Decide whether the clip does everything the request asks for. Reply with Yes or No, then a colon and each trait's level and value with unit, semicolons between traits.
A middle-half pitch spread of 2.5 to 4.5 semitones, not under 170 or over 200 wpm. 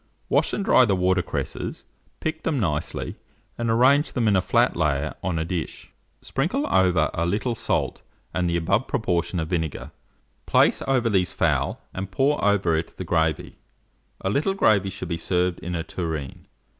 No: wide, 5.5 semitones; average, 180 wpm